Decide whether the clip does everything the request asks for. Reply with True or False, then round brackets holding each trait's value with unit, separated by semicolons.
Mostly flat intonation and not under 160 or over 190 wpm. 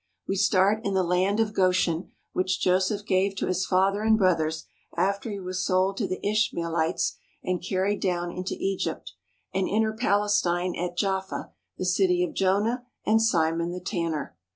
True (2.1 semitones; 170 wpm)